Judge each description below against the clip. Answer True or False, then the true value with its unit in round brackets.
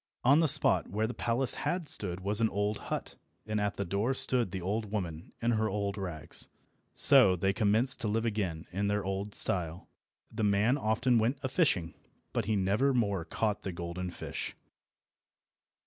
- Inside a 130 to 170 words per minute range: False (180 wpm)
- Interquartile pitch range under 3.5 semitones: True (3.1 semitones)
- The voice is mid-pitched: False (105 Hz)